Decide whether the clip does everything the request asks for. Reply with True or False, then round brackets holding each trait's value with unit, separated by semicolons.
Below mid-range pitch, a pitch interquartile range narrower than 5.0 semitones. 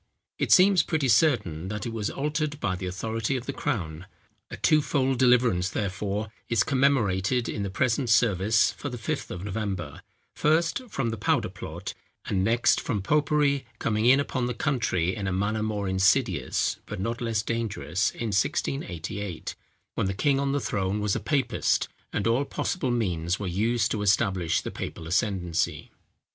False (110 Hz; 5.3 semitones)